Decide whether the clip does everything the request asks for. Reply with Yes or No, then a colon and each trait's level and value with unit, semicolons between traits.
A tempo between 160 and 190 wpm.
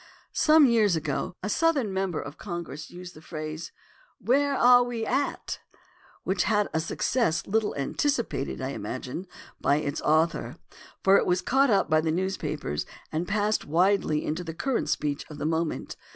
Yes: average, 165 wpm